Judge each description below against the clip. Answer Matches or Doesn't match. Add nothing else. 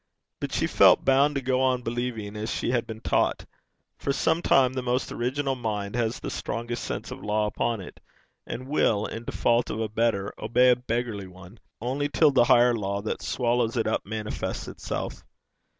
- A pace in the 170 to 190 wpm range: Matches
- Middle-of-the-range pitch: Doesn't match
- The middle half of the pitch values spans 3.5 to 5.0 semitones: Doesn't match